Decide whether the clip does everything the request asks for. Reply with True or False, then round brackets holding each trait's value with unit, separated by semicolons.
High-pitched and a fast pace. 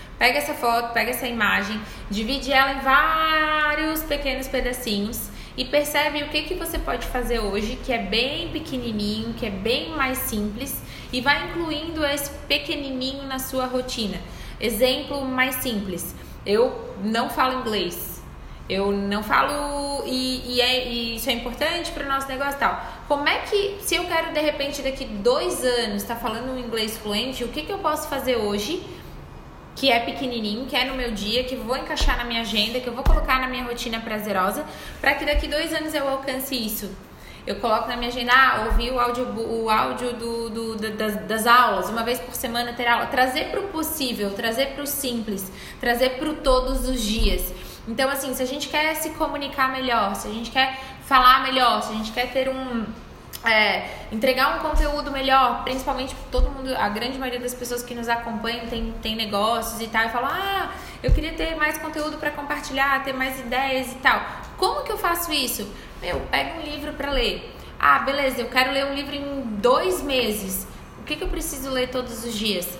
True (255 Hz; 195 wpm)